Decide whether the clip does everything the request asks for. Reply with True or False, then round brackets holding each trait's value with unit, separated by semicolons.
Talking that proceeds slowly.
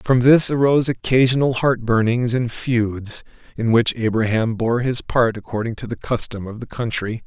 False (175 wpm)